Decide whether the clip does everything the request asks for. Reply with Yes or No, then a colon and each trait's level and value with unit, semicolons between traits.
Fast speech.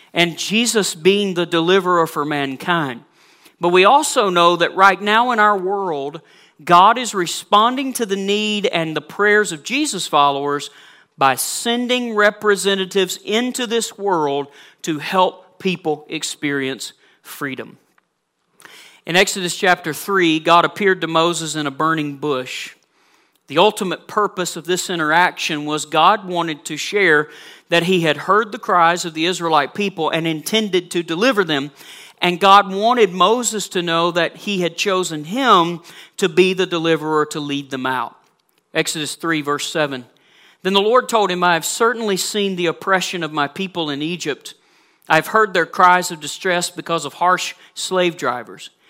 No: average, 160 wpm